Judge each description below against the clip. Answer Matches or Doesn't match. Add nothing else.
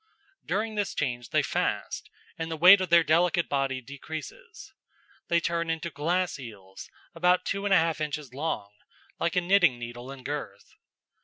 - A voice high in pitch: Doesn't match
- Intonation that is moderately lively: Matches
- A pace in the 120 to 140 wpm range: Doesn't match